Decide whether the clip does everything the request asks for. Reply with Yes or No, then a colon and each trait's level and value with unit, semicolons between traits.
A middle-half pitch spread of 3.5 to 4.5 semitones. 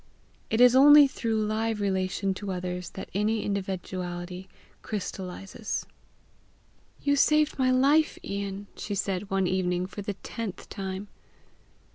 No: average, 3.1 semitones